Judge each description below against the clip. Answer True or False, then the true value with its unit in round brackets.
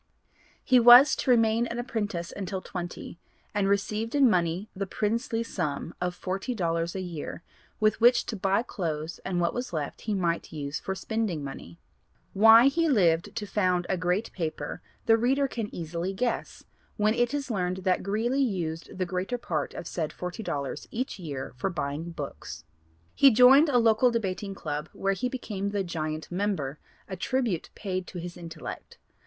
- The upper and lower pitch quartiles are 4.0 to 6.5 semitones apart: True (5.1 semitones)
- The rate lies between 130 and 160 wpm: False (175 wpm)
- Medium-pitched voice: False (195 Hz)